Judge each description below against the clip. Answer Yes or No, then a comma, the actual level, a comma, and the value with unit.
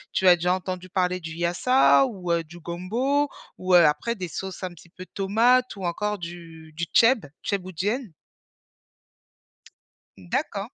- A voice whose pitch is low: No, medium, 185 Hz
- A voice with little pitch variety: No, average, 3.4 semitones